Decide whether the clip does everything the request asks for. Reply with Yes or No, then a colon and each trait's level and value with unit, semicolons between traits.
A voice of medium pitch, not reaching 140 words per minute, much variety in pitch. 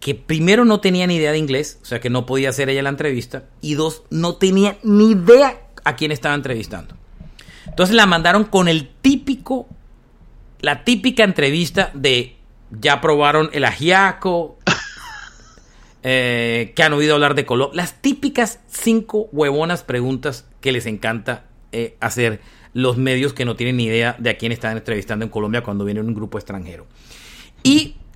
No: medium, 145 Hz; average, 165 wpm; wide, 7.0 semitones